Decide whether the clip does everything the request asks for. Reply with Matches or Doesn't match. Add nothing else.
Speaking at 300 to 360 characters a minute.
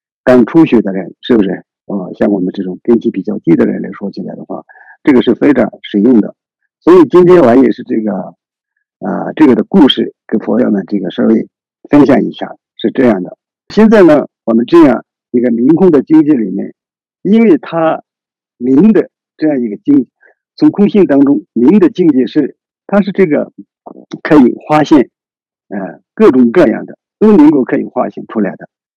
Doesn't match